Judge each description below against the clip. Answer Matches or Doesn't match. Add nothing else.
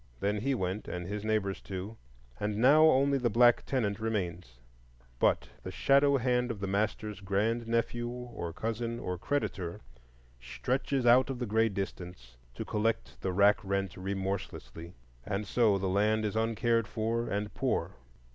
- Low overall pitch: Matches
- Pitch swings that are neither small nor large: Matches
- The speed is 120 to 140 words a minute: Doesn't match